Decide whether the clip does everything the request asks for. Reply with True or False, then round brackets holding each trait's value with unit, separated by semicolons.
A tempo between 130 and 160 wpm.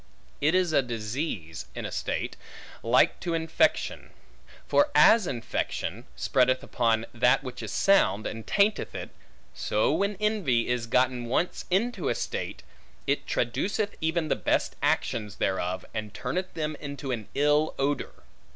True (145 wpm)